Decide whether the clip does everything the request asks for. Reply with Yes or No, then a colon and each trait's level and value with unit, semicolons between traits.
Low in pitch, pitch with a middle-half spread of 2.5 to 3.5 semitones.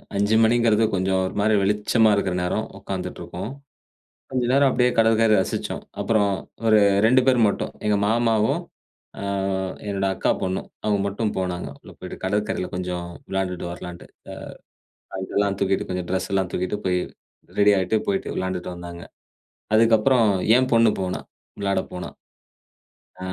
Yes: low, 100 Hz; average, 3.2 semitones